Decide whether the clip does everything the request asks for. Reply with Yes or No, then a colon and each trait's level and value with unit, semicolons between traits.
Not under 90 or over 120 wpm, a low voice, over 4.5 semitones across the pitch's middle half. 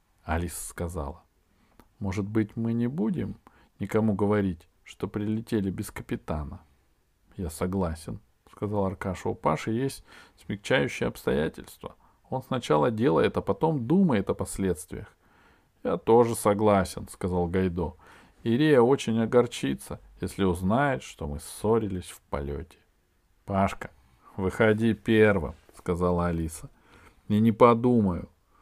No: slow, 110 wpm; very low, 95 Hz; average, 3.9 semitones